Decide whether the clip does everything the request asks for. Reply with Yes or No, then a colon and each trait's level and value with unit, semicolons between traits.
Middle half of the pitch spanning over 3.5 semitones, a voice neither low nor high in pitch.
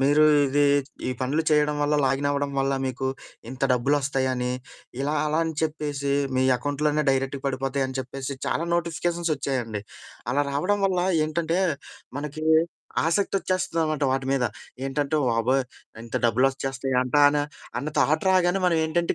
No: average, 2.8 semitones; medium, 145 Hz